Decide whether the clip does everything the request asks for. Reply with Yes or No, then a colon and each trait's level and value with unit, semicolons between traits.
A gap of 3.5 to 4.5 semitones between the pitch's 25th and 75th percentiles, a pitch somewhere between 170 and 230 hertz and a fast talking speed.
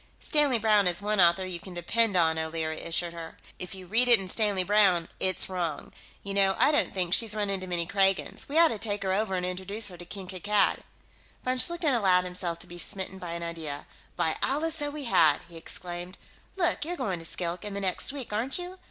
Yes: average, 4.1 semitones; high, 190 Hz; fast, 225 wpm